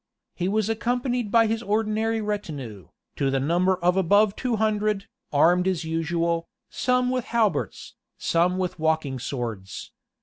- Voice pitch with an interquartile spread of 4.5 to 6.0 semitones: Yes, average, 5.3 semitones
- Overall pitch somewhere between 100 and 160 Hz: No, high, 190 Hz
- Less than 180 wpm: Yes, average, 140 wpm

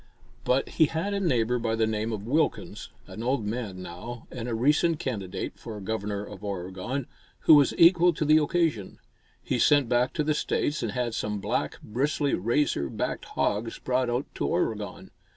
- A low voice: Yes, low, 120 Hz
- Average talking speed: Yes, average, 180 wpm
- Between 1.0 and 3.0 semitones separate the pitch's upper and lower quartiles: No, wide, 5.6 semitones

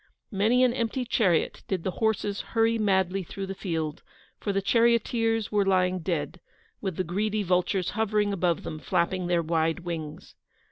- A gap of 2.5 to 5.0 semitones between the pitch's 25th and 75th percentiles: Yes, average, 3.8 semitones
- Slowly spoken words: No, average, 160 wpm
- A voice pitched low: No, high, 195 Hz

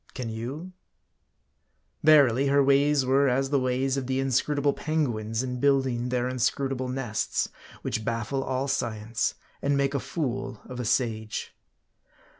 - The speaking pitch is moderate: No, low, 130 Hz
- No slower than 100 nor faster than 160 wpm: Yes, average, 140 wpm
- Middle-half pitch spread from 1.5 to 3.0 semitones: Yes, narrow, 2.4 semitones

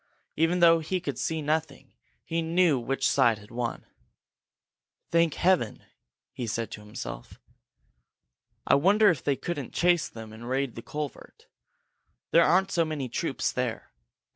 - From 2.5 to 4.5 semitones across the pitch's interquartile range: No, wide, 5.5 semitones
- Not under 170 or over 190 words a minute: No, average, 145 wpm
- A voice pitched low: No, medium, 150 Hz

